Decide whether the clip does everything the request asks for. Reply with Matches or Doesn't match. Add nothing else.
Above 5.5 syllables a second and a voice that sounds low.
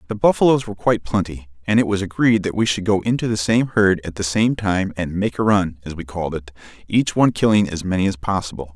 Matches